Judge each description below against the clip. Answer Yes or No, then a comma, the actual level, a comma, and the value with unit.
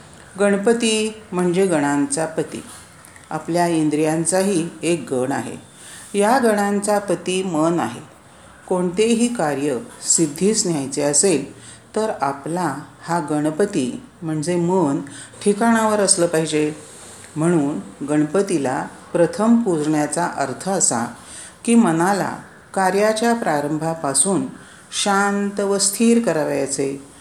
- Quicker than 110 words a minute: No, average, 95 wpm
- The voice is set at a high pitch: No, medium, 170 Hz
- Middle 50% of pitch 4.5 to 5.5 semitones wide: Yes, average, 5.0 semitones